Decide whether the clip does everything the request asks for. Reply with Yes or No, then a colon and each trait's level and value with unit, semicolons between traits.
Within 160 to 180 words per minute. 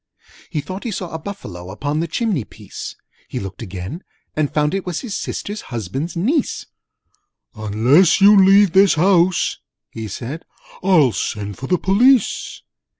No: average, 150 wpm